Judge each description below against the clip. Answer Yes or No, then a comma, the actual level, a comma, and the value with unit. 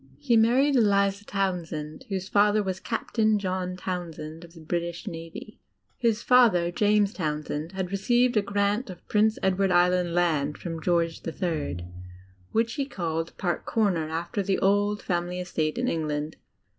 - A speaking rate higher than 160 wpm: No, average, 155 wpm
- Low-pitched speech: No, medium, 185 Hz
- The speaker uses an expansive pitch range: No, average, 3.8 semitones